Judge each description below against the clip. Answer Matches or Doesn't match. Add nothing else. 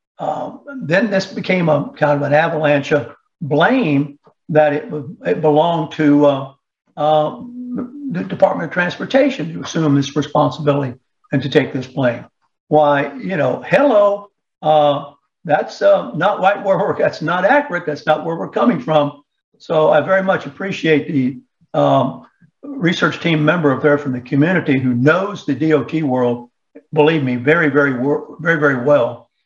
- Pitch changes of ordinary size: Matches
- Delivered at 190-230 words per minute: Doesn't match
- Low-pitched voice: Doesn't match